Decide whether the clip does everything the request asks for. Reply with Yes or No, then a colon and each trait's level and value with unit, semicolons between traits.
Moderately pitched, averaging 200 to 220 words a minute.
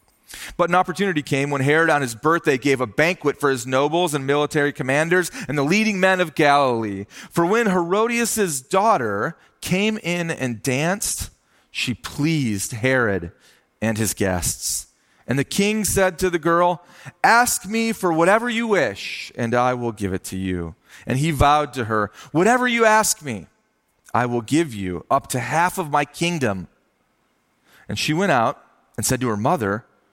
No: medium, 150 Hz; average, 170 wpm